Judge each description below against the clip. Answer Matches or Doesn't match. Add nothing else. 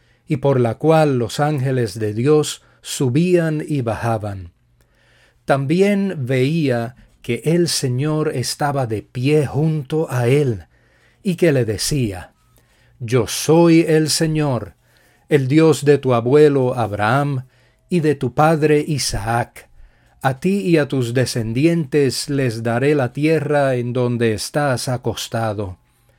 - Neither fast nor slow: Doesn't match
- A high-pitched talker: Doesn't match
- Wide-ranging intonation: Doesn't match